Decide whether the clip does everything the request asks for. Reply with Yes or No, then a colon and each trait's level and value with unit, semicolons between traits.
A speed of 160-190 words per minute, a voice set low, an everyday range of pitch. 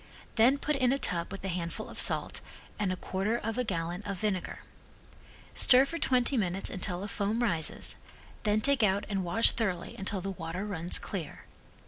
No: average, 185 wpm; high, 200 Hz; average, 4.1 semitones